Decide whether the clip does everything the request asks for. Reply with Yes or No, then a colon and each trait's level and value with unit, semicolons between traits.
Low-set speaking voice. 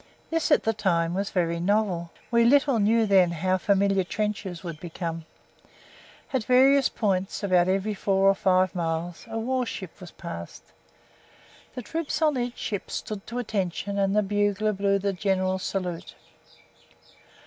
No: high, 195 Hz